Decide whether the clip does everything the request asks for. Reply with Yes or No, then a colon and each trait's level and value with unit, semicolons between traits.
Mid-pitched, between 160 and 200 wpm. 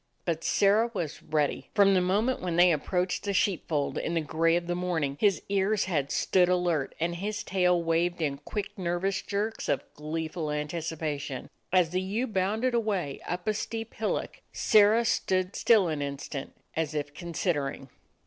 Yes: medium, 175 Hz; average, 170 wpm